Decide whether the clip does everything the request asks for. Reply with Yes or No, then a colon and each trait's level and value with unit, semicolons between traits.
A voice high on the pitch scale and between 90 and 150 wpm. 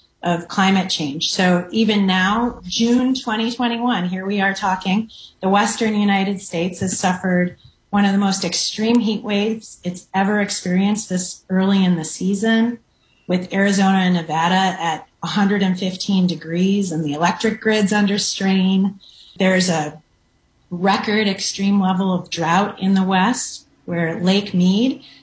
Yes: high, 195 Hz; average, 140 wpm